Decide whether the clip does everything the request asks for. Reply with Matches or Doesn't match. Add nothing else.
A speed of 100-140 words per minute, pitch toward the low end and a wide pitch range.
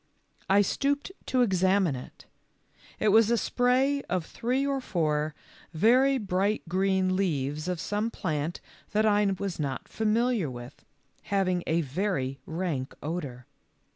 Doesn't match